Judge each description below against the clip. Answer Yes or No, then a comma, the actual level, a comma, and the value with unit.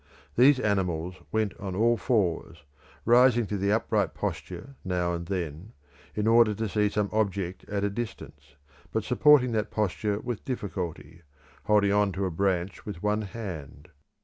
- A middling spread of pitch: Yes, average, 3.3 semitones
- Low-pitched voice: Yes, low, 105 Hz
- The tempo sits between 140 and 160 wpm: Yes, average, 155 wpm